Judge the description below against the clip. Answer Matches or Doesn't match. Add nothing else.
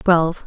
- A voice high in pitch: Doesn't match